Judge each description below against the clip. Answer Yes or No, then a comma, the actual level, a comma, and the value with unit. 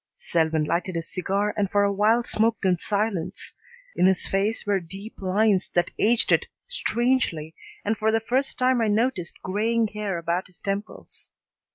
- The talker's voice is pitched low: No, high, 205 Hz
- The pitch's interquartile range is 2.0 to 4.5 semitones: Yes, average, 3.3 semitones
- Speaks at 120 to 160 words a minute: No, average, 170 wpm